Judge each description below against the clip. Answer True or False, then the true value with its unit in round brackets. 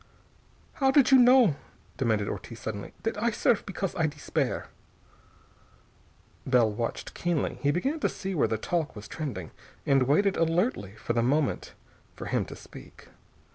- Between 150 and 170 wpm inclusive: True (155 wpm)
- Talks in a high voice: False (155 Hz)